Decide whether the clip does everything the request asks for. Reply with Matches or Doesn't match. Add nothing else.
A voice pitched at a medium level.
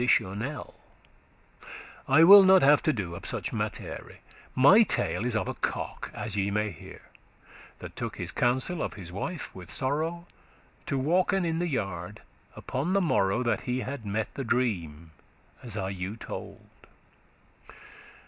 Doesn't match